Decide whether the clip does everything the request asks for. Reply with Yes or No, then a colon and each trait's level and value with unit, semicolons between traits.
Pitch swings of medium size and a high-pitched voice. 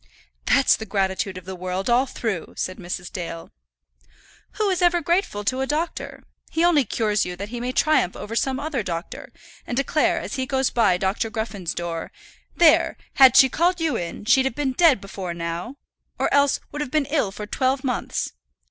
No: wide, 6.9 semitones; high, 240 Hz